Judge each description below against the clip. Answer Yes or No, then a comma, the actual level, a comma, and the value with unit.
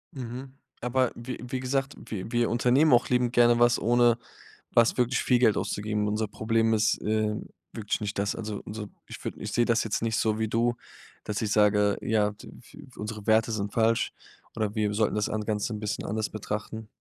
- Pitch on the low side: Yes, low, 110 Hz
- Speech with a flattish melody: Yes, narrow, 2.1 semitones